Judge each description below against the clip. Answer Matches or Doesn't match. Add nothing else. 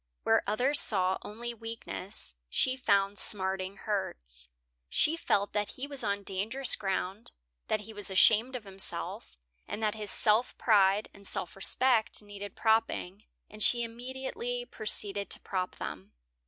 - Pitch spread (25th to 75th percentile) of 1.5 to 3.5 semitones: Matches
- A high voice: Matches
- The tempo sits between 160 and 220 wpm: Doesn't match